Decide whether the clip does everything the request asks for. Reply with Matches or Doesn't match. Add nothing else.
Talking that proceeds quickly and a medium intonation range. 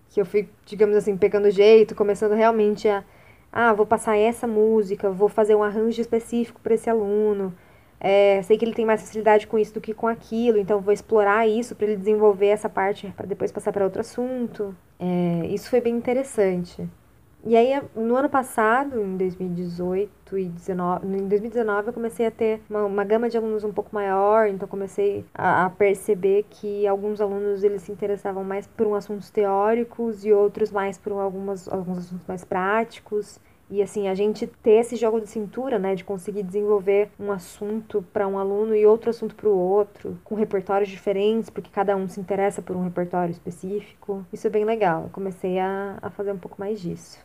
Doesn't match